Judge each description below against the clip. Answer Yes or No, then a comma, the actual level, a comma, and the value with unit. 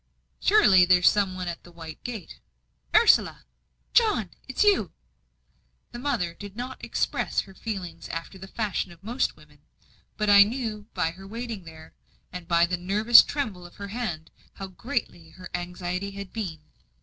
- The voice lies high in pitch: Yes, high, 195 Hz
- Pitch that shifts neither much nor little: Yes, average, 4.2 semitones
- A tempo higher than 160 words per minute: Yes, average, 170 wpm